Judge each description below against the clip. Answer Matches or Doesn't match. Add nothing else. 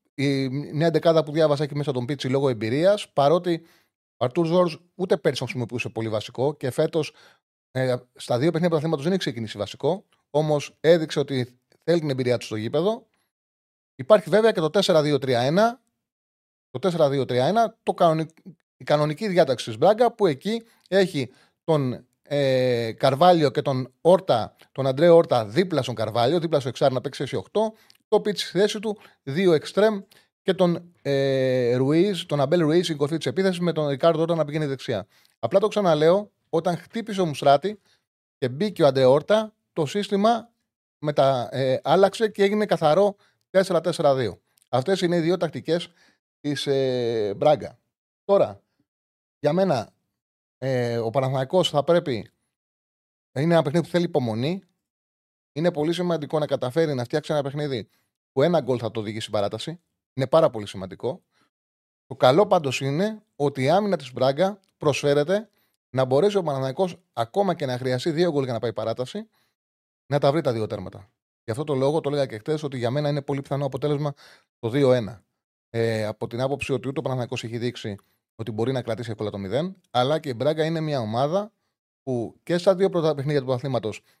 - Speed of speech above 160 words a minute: Matches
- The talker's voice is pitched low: Doesn't match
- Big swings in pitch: Matches